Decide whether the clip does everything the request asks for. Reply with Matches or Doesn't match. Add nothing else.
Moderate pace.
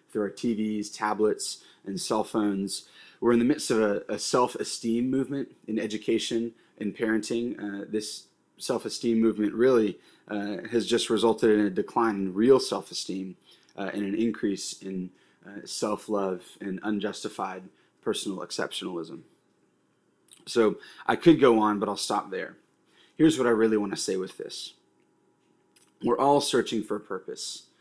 Matches